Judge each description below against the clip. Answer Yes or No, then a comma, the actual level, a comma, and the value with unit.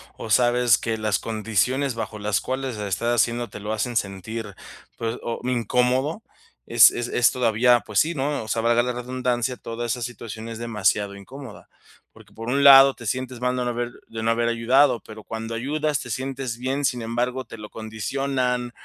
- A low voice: Yes, low, 120 Hz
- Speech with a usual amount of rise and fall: No, narrow, 2.3 semitones